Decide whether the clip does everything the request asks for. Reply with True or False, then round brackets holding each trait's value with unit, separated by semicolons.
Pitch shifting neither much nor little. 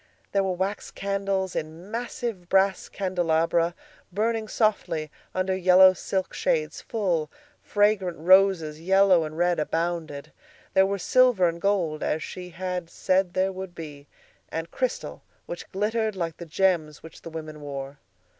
True (3.2 semitones)